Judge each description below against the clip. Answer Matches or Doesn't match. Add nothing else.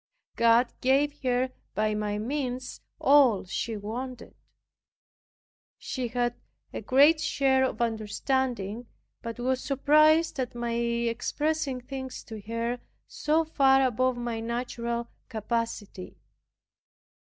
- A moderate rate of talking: Doesn't match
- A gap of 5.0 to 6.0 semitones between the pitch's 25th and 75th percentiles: Doesn't match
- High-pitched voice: Matches